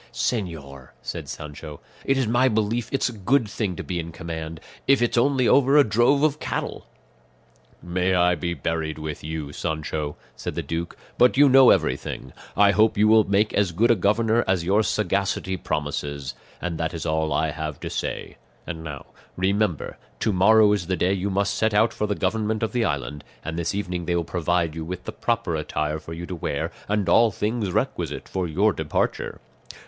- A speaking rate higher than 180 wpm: Yes, average, 195 wpm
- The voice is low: Yes, very low, 95 Hz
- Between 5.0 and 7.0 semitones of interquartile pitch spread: Yes, average, 5.3 semitones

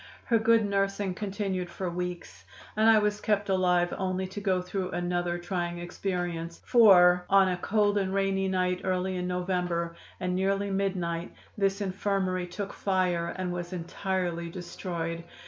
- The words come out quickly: No, average, 150 wpm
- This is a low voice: No, medium, 185 Hz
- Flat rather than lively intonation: Yes, narrow, 1.9 semitones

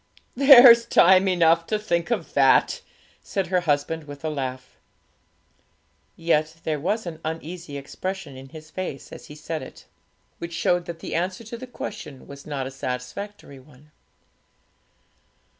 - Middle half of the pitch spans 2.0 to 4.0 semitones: No, average, 4.6 semitones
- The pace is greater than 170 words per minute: No, average, 150 wpm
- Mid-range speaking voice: Yes, medium, 165 Hz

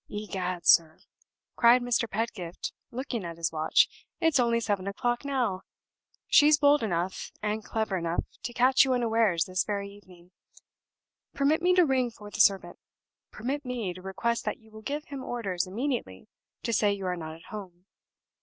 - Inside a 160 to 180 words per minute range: Yes, average, 170 wpm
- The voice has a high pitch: Yes, high, 215 Hz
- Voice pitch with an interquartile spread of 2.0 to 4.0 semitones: No, average, 5.1 semitones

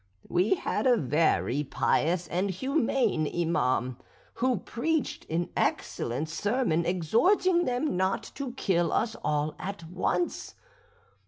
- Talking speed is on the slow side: Yes, slow, 115 wpm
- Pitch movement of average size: No, wide, 7.7 semitones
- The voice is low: No, medium, 185 Hz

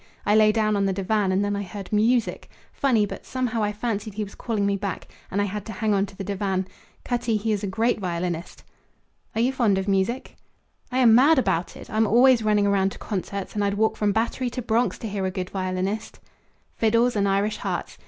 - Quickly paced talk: Yes, fast, 225 wpm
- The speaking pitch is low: No, high, 210 Hz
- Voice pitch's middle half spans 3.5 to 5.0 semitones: No, narrow, 2.4 semitones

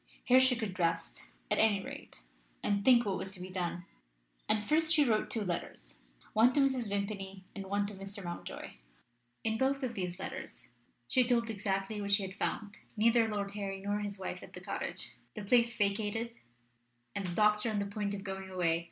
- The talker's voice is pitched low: No, high, 205 Hz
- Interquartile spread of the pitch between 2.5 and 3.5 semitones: Yes, average, 2.8 semitones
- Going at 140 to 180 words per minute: No, average, 195 wpm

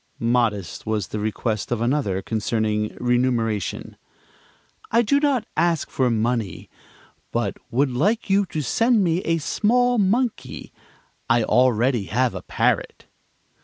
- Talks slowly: Yes, slow, 130 wpm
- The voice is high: No, low, 125 Hz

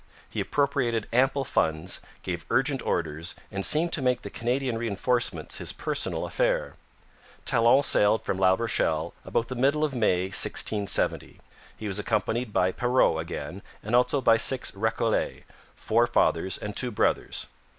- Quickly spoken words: No, average, 150 wpm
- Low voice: Yes, low, 115 Hz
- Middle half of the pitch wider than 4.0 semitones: Yes, average, 4.6 semitones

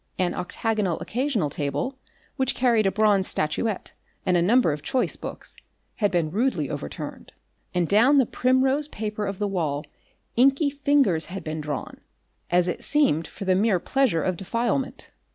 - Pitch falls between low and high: No, high, 205 Hz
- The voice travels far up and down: Yes, wide, 6.8 semitones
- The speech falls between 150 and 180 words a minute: Yes, average, 160 wpm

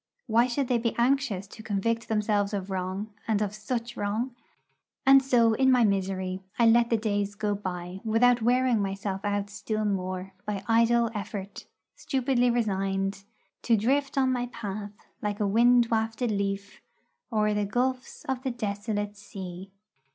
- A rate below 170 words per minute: Yes, average, 160 wpm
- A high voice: Yes, high, 215 Hz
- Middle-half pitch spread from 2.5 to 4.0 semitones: Yes, average, 3.1 semitones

